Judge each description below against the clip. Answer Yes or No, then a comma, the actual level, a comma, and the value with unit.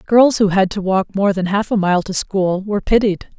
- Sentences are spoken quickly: Yes, fast, 250 wpm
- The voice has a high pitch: Yes, high, 195 Hz